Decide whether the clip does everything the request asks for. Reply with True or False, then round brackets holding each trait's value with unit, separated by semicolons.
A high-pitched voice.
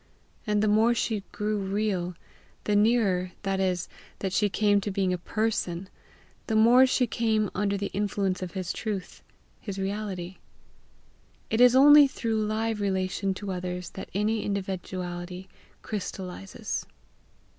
True (200 Hz)